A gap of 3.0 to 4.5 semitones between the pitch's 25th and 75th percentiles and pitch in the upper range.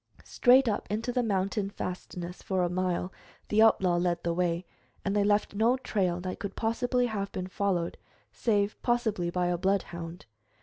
Yes: average, 3.5 semitones; high, 195 Hz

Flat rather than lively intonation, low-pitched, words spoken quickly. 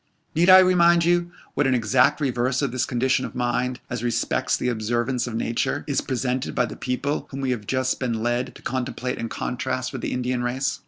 Yes: narrow, 1.7 semitones; low, 125 Hz; fast, 210 wpm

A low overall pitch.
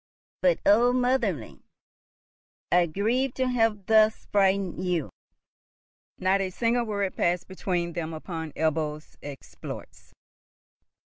No: high, 190 Hz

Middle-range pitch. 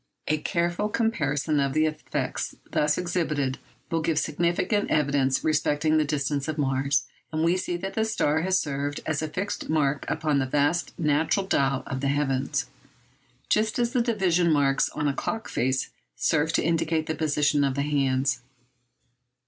Yes: medium, 150 Hz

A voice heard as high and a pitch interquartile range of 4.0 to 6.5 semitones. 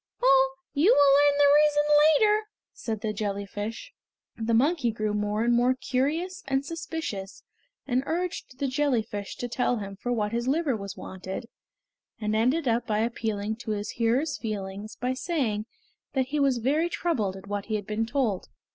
Yes: high, 245 Hz; average, 5.2 semitones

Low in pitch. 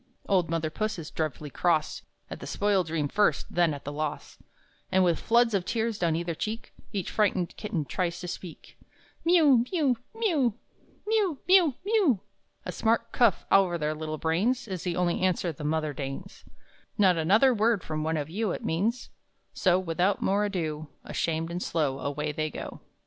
No: medium, 180 Hz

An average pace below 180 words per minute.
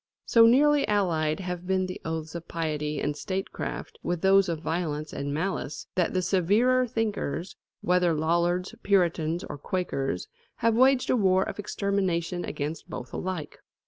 Yes: average, 150 wpm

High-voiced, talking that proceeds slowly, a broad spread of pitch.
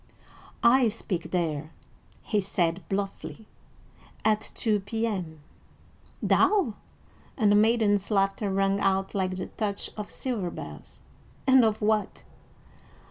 No: high, 205 Hz; slow, 115 wpm; narrow, 2.5 semitones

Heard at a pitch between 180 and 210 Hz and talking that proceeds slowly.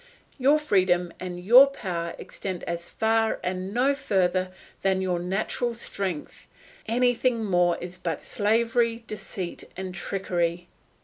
Yes: high, 190 Hz; slow, 125 wpm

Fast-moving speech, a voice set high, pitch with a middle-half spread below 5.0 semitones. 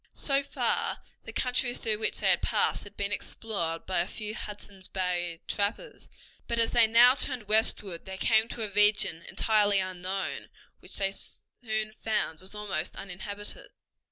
No: average, 160 wpm; high, 205 Hz; average, 2.7 semitones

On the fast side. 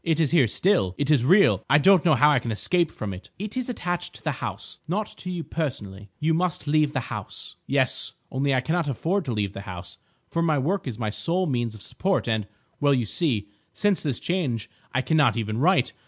Yes: fast, 220 wpm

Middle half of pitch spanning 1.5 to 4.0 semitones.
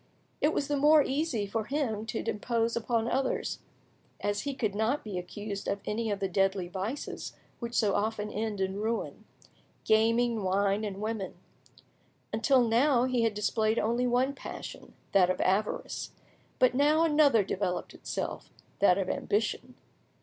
Yes: average, 3.6 semitones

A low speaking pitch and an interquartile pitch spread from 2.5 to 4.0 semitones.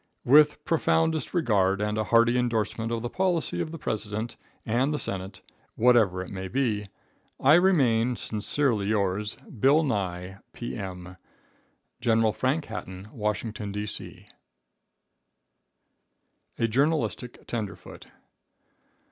No: low, 115 Hz; average, 4.7 semitones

